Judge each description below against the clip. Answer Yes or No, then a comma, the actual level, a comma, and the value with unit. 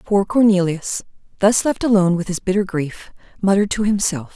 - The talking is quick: No, average, 165 wpm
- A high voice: Yes, high, 195 Hz